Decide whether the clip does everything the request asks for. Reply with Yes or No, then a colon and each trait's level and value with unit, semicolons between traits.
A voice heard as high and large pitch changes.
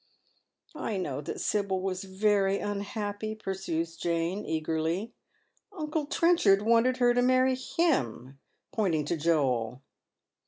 Yes: high, 195 Hz; wide, 6.0 semitones